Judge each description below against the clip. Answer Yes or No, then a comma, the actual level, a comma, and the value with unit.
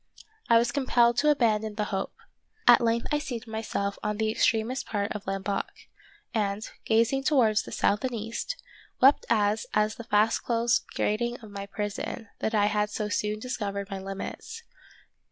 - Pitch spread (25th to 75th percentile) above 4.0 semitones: No, narrow, 2.4 semitones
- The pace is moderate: Yes, average, 170 wpm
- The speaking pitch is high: Yes, high, 220 Hz